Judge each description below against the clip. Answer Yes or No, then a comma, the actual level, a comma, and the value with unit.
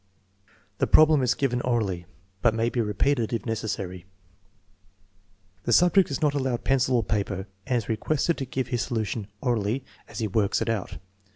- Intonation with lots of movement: No, average, 3.8 semitones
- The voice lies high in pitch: No, low, 120 Hz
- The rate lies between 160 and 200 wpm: Yes, average, 170 wpm